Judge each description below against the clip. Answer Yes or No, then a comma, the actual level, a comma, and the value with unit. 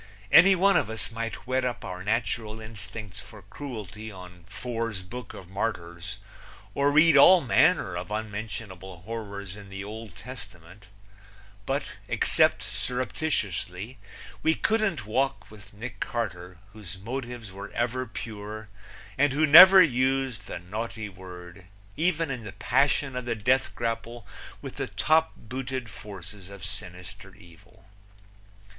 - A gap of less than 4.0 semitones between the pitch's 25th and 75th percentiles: No, average, 4.7 semitones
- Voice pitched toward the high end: No, low, 110 Hz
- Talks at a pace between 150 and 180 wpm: No, average, 140 wpm